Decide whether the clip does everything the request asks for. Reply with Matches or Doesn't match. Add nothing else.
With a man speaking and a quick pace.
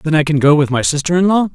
Matches